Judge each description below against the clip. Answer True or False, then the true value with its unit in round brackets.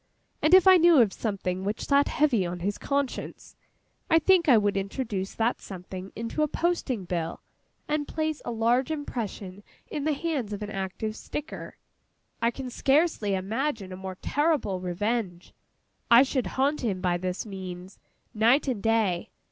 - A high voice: True (225 Hz)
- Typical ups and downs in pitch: False (6.9 semitones)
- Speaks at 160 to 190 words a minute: True (165 wpm)